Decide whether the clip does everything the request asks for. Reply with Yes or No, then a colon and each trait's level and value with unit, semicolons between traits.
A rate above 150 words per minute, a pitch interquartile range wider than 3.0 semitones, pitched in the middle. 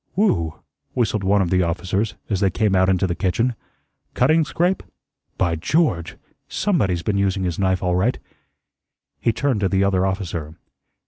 No: average, 165 wpm; average, 3.5 semitones; very low, 95 Hz